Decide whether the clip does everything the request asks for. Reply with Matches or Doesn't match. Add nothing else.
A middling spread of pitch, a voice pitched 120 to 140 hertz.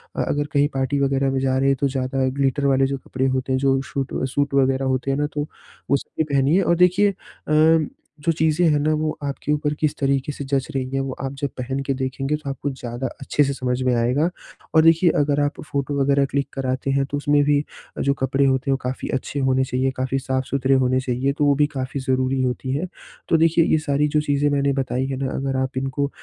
Doesn't match